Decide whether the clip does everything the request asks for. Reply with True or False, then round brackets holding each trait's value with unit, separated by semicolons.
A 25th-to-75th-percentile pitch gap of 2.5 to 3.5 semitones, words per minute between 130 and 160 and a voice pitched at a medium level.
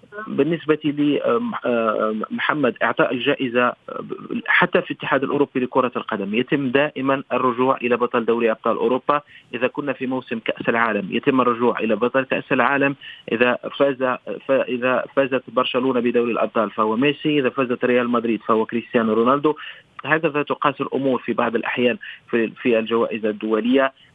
False (2.9 semitones; 135 wpm; 125 Hz)